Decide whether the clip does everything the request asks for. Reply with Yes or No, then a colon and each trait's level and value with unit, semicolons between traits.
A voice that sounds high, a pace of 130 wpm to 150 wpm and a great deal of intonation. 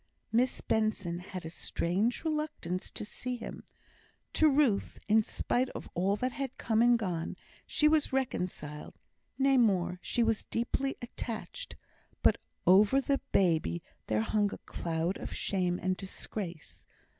Yes: high, 215 Hz; average, 145 wpm; wide, 5.9 semitones